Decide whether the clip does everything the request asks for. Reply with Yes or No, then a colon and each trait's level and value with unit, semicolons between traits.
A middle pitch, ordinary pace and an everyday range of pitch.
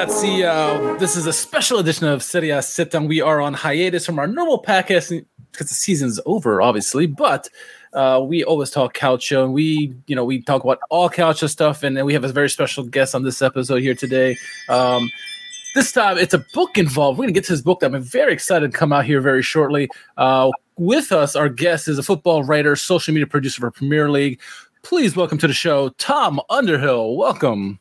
No: medium, 150 Hz; fast, 220 wpm; average, 4.5 semitones